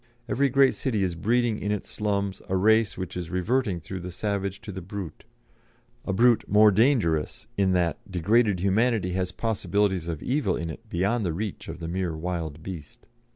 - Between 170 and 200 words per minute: Yes, average, 185 wpm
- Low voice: Yes, very low, 95 Hz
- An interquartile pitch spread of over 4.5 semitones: No, average, 3.7 semitones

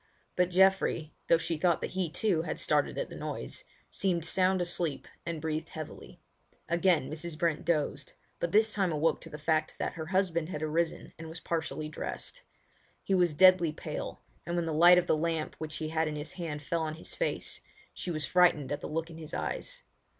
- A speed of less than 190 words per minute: No, average, 200 wpm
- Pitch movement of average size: No, narrow, 2.3 semitones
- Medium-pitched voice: Yes, medium, 165 Hz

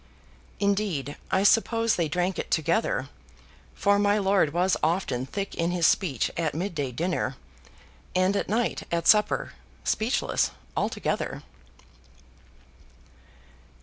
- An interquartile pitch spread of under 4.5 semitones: Yes, average, 4.0 semitones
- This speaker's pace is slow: Yes, slow, 115 wpm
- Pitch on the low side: No, medium, 185 Hz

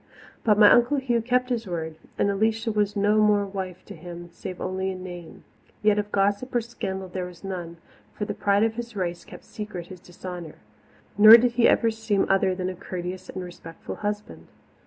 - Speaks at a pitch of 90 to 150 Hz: No, high, 200 Hz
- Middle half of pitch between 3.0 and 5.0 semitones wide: Yes, average, 3.3 semitones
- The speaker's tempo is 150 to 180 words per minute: No, average, 200 wpm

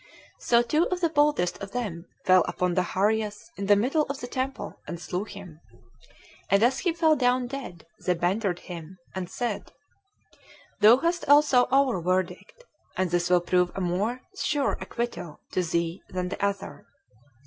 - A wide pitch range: Yes, wide, 6.3 semitones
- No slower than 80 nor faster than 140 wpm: No, average, 165 wpm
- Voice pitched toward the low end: No, high, 205 Hz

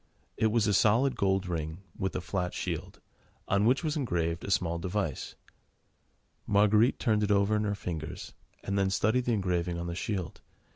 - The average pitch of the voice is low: Yes, low, 100 Hz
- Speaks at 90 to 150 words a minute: No, average, 180 wpm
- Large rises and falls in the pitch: No, average, 3.4 semitones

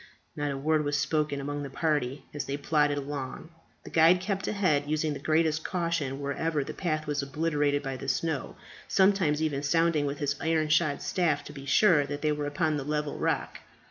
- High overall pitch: No, medium, 150 Hz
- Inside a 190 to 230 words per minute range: Yes, average, 200 wpm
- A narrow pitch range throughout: Yes, narrow, 2.0 semitones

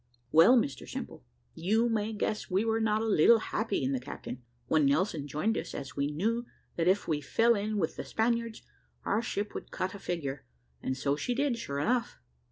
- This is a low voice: No, high, 205 Hz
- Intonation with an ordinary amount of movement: No, wide, 7.2 semitones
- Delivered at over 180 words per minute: Yes, average, 200 wpm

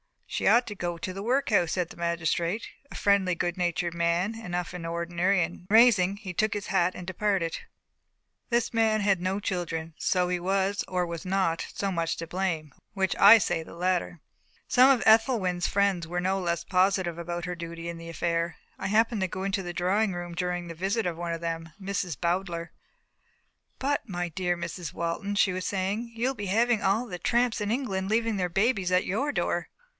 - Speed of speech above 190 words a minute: Yes, average, 200 wpm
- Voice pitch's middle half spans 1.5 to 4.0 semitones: Yes, average, 2.9 semitones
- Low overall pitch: No, medium, 185 Hz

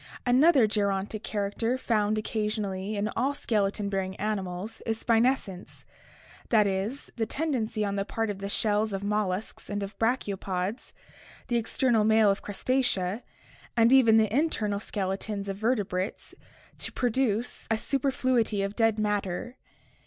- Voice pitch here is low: No, high, 215 Hz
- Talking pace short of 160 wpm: Yes, average, 140 wpm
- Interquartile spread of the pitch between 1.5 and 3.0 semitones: Yes, narrow, 2.6 semitones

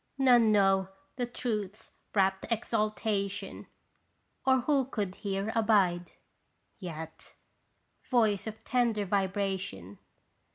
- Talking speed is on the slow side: Yes, slow, 90 wpm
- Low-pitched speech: No, high, 205 Hz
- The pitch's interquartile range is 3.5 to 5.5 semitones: No, average, 3.1 semitones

